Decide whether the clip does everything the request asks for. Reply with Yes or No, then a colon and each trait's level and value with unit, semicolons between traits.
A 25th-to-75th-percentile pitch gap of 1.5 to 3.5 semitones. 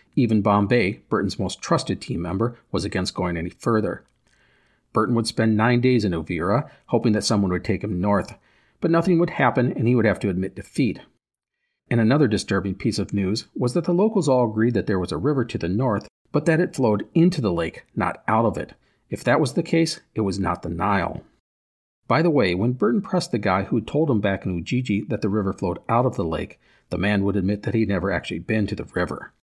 No: average, 4.4 semitones